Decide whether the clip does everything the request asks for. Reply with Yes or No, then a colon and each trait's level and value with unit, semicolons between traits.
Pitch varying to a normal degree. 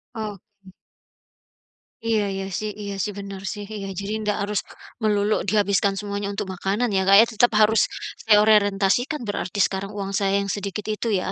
No: narrow, 1.3 semitones